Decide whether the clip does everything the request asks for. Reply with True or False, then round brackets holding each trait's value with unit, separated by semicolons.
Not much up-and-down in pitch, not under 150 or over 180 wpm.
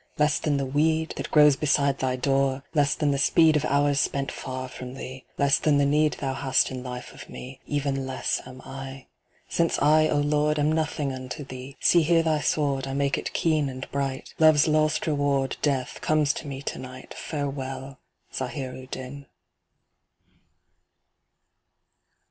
True (2.2 semitones; 170 wpm)